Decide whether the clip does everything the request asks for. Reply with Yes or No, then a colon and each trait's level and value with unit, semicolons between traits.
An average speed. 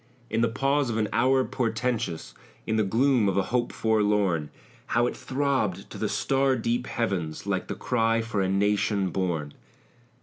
Yes: average, 170 wpm